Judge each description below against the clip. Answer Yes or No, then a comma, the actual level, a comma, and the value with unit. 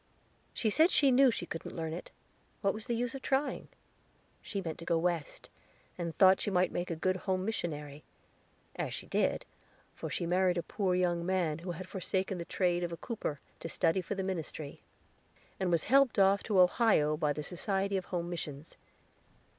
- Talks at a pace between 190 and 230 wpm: Yes, average, 195 wpm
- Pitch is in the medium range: Yes, medium, 180 Hz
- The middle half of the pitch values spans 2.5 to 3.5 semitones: Yes, average, 2.9 semitones